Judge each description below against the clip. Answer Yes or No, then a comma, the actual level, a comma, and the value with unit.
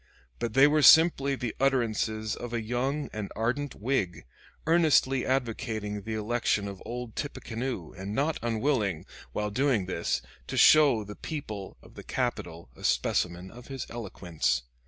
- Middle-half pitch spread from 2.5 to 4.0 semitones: No, average, 4.6 semitones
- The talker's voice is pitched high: No, low, 115 Hz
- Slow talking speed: No, average, 150 wpm